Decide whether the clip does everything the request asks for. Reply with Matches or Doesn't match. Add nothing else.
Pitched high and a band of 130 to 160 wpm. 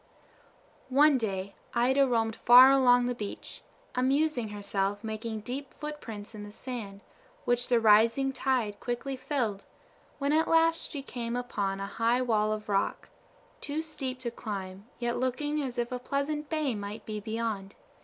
Matches